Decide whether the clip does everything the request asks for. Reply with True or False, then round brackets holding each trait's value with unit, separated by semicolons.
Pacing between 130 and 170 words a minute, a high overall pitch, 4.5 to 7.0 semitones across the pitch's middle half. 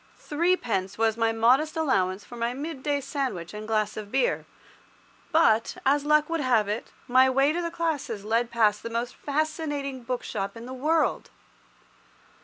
True (160 wpm; 255 Hz; 5.1 semitones)